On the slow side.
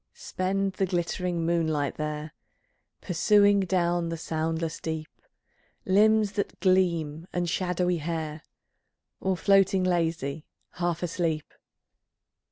Yes: slow, 100 wpm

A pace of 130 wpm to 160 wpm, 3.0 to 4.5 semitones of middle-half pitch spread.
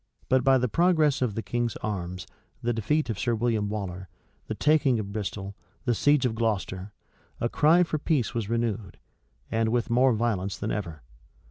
No: average, 175 wpm; average, 4.1 semitones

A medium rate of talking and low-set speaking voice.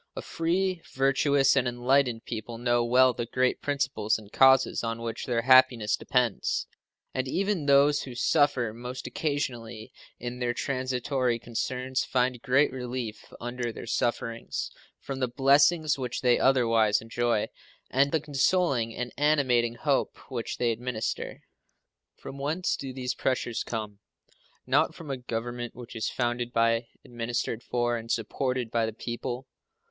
Yes: average, 145 wpm; low, 125 Hz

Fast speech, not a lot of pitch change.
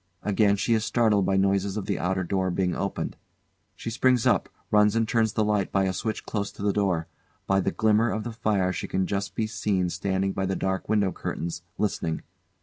Yes: fast, 215 wpm; narrow, 2.3 semitones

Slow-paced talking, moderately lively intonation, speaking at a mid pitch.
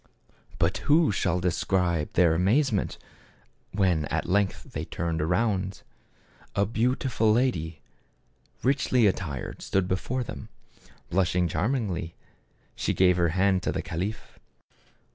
No: slow, 120 wpm; average, 4.2 semitones; very low, 95 Hz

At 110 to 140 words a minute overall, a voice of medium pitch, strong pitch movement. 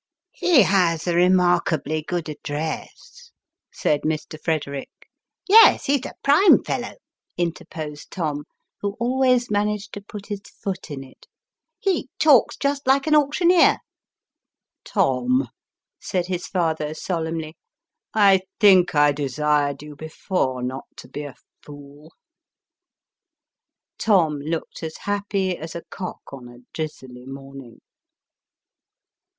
Yes: slow, 135 wpm; medium, 170 Hz; wide, 5.8 semitones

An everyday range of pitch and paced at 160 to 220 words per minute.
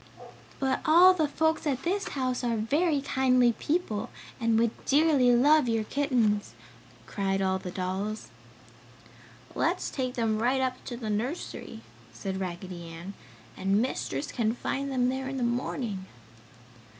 No: average, 4.8 semitones; average, 145 wpm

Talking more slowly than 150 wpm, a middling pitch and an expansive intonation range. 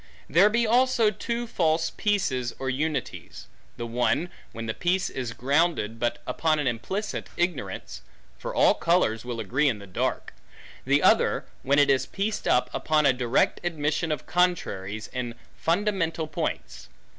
No: average, 155 wpm; medium, 150 Hz; wide, 6.5 semitones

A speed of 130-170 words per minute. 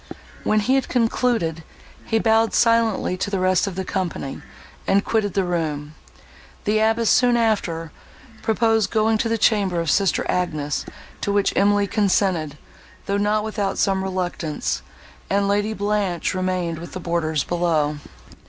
Yes: average, 150 wpm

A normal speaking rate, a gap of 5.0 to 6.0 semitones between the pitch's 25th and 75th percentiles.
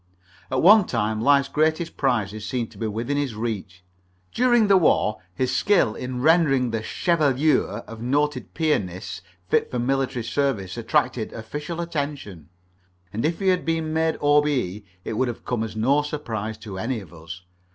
Yes: average, 165 wpm; wide, 5.5 semitones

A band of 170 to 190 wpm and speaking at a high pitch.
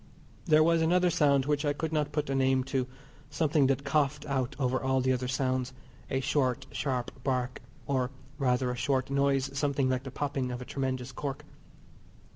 No: average, 185 wpm; low, 135 Hz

